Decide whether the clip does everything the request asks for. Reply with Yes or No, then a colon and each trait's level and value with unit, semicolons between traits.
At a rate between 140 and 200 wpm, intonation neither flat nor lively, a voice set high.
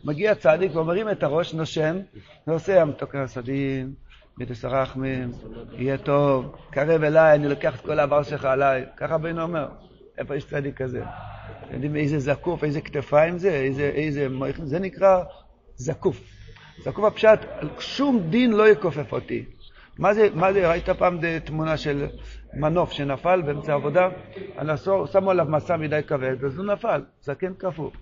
No: average, 145 wpm; average, 4.6 semitones; medium, 150 Hz